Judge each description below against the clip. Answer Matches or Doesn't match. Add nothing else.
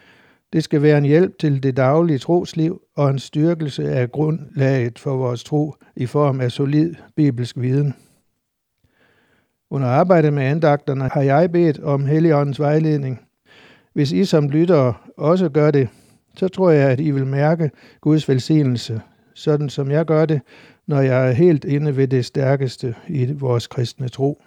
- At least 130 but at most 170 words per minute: Matches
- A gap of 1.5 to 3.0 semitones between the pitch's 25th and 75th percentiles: Matches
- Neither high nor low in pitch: Matches